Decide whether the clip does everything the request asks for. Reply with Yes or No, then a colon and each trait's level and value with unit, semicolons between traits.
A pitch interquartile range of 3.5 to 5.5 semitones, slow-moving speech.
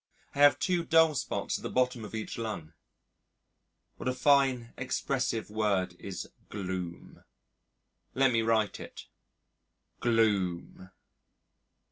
Yes: average, 4.7 semitones; slow, 115 wpm